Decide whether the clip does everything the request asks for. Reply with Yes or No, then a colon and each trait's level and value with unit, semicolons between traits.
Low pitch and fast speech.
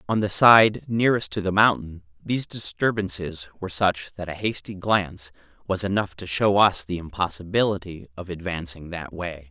No: very low, 90 Hz; average, 165 wpm